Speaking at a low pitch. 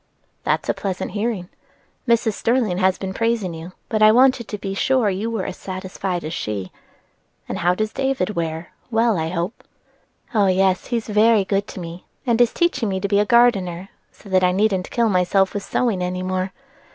No: high, 195 Hz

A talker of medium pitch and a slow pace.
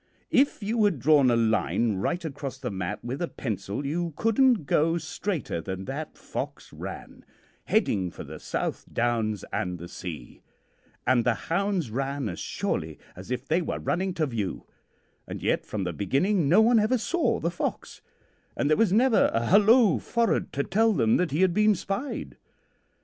No: medium, 150 Hz; average, 175 wpm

